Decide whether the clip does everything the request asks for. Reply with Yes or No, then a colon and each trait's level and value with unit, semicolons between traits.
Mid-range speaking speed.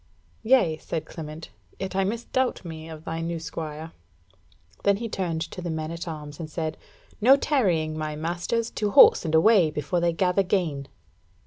Yes: average, 175 wpm